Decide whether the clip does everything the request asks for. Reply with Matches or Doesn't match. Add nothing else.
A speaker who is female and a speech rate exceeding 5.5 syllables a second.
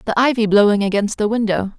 Matches